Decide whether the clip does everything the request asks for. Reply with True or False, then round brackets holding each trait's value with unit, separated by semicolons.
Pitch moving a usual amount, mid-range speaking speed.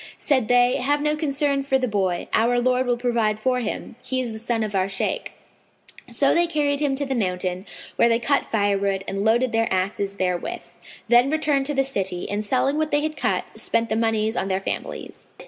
False (5.0 semitones; 210 wpm)